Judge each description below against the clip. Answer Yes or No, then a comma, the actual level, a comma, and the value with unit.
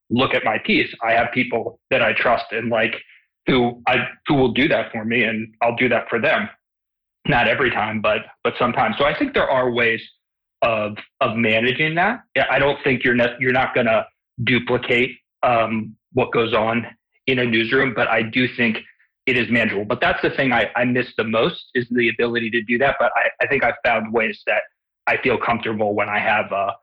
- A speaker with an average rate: No, fast, 215 wpm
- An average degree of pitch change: No, narrow, 1.8 semitones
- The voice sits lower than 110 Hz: No, low, 120 Hz